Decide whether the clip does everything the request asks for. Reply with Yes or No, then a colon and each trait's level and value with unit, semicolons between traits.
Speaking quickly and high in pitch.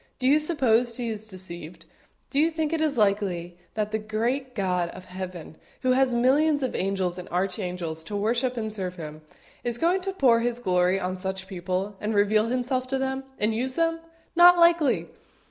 No: average, 185 wpm; high, 220 Hz